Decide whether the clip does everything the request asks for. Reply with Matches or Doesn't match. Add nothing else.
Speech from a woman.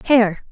Matches